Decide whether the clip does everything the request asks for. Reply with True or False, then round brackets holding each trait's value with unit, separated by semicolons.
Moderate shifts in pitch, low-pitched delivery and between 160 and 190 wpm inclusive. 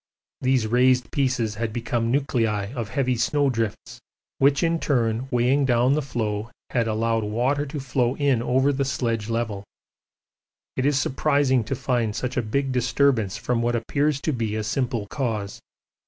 True (3.1 semitones; 125 Hz; 165 wpm)